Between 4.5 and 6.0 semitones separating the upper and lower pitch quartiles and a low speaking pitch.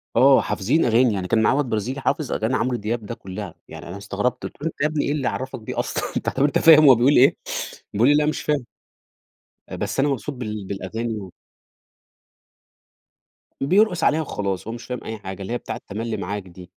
Yes: average, 5.1 semitones; low, 120 Hz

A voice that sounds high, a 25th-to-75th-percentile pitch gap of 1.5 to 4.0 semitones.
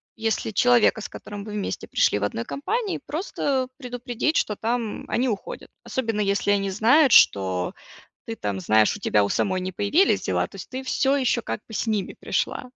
No: high, 220 Hz; average, 4.6 semitones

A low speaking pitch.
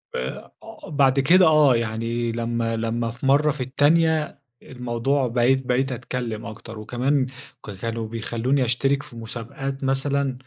Yes: low, 125 Hz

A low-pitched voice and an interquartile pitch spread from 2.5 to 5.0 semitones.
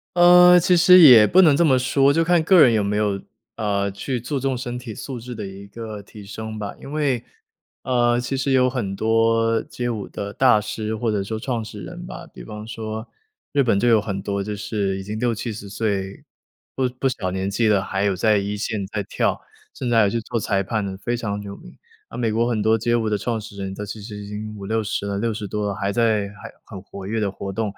Yes: low, 110 Hz; average, 3.2 semitones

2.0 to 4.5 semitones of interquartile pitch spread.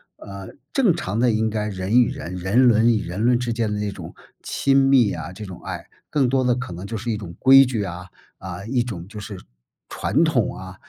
Yes: average, 4.1 semitones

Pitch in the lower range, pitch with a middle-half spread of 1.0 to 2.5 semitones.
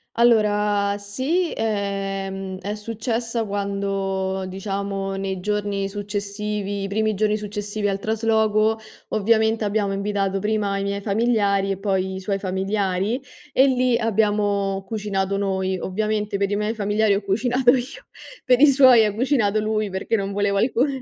No: high, 205 Hz; narrow, 1.8 semitones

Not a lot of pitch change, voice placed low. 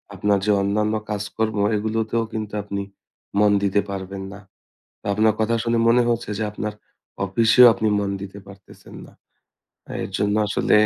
Yes: narrow, 1.6 semitones; low, 105 Hz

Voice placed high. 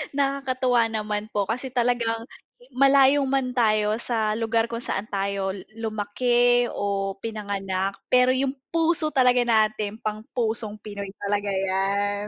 Yes: high, 225 Hz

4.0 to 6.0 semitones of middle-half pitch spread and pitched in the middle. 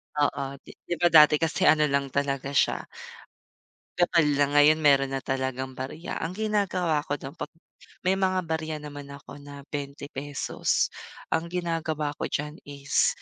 No: narrow, 2.5 semitones; medium, 150 Hz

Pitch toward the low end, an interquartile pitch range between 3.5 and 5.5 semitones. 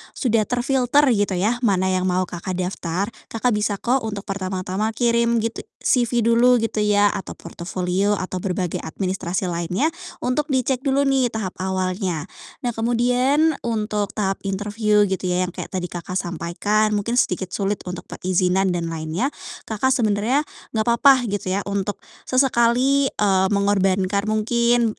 No: high, 205 Hz; average, 4.2 semitones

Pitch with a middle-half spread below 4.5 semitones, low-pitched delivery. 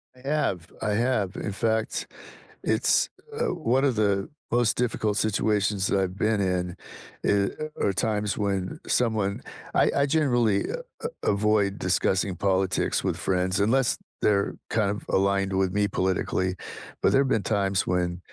Yes: average, 2.8 semitones; low, 100 Hz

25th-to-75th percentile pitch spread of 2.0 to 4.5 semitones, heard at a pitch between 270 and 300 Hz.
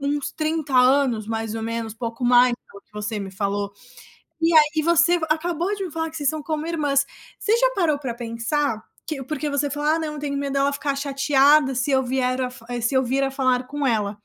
Yes: average, 3.9 semitones; very high, 275 Hz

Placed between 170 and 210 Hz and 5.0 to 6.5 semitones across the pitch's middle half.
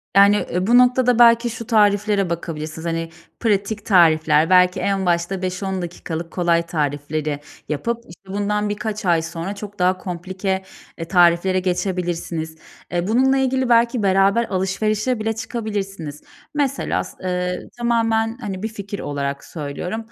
No: high, 190 Hz; average, 4.3 semitones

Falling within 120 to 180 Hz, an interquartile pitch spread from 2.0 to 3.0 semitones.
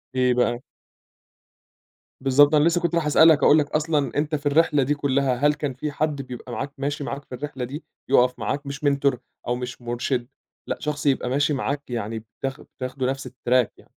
Yes: medium, 140 Hz; average, 2.7 semitones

